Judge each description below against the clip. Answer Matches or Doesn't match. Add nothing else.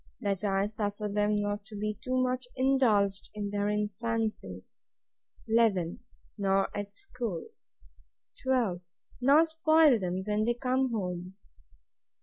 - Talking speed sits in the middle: Doesn't match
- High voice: Matches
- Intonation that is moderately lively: Matches